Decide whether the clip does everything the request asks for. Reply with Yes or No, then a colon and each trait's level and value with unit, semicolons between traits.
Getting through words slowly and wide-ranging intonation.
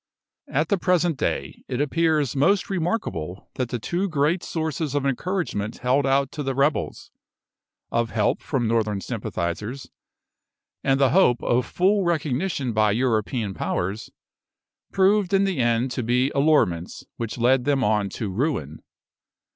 No: average, 145 wpm; wide, 5.7 semitones